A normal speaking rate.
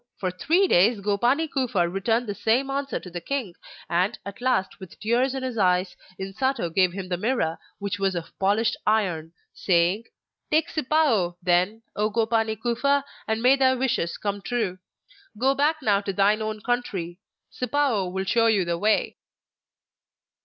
Yes: average, 165 wpm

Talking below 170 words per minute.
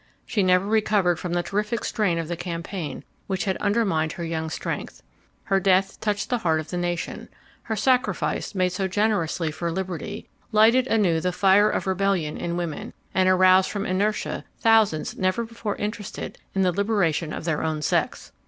No: average, 175 wpm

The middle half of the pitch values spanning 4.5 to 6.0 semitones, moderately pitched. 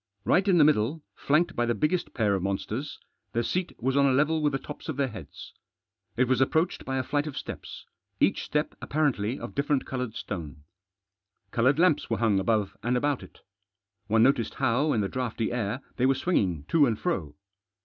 No: average, 5.0 semitones; low, 130 Hz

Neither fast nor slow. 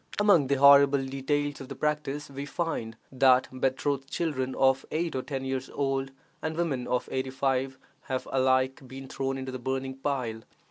Yes: average, 175 wpm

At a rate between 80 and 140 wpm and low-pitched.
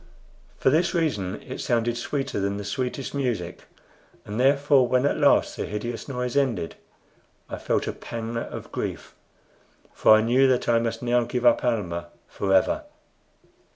No: average, 155 wpm; low, 120 Hz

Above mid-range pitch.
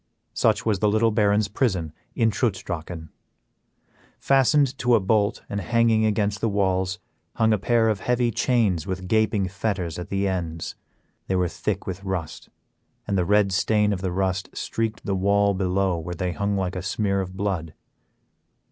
No: low, 100 Hz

